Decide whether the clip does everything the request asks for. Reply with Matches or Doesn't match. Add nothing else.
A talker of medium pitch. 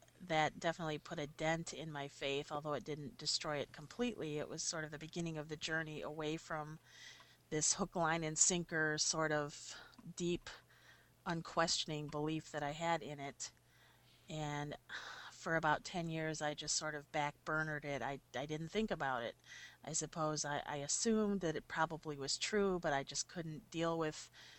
Matches